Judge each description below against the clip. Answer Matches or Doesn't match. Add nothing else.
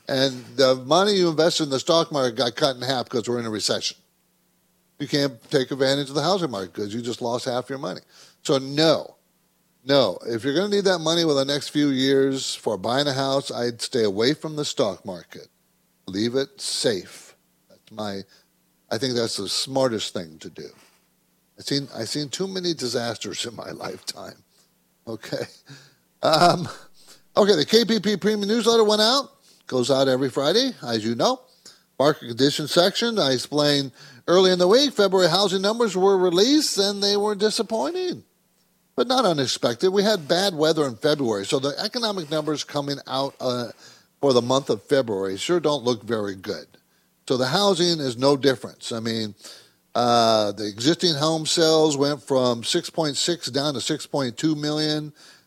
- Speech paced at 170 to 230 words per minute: Matches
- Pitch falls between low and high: Matches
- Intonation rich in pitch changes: Matches